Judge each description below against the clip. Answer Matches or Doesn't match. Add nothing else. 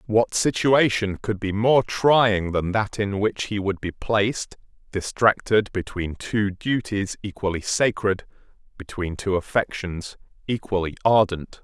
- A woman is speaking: Doesn't match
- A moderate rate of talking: Doesn't match